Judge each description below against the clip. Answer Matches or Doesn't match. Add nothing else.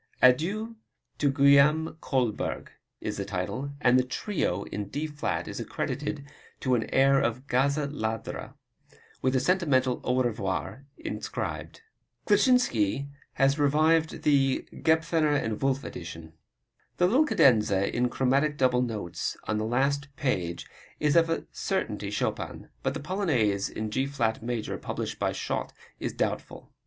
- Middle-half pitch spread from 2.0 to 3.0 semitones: Doesn't match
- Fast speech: Doesn't match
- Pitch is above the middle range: Doesn't match